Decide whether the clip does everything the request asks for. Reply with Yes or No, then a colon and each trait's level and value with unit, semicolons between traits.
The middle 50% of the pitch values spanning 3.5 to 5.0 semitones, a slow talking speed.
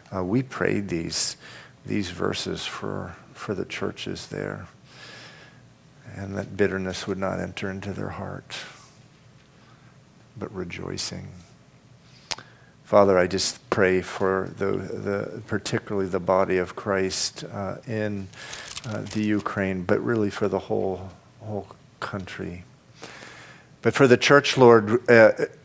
Yes: average, 4.5 semitones; slow, 120 wpm